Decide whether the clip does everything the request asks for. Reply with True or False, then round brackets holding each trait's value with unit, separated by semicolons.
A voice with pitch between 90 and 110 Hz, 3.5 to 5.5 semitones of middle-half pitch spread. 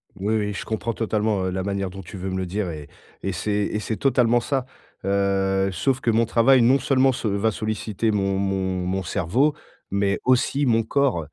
False (105 Hz; 3.1 semitones)